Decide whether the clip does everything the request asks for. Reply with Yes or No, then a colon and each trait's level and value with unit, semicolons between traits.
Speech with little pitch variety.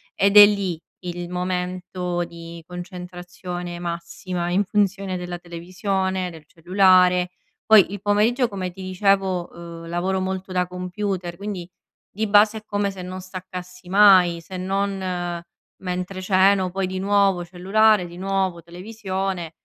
Yes: narrow, 1.8 semitones